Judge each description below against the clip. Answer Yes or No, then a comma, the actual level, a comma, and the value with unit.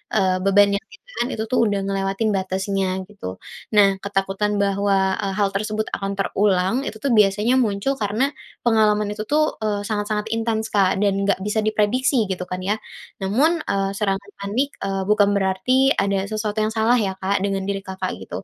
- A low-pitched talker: No, high, 205 Hz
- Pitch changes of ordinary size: No, narrow, 1.8 semitones